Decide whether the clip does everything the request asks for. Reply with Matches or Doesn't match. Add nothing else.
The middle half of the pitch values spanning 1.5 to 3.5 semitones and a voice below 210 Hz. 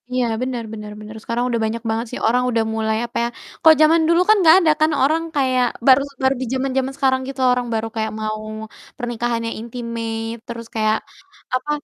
Doesn't match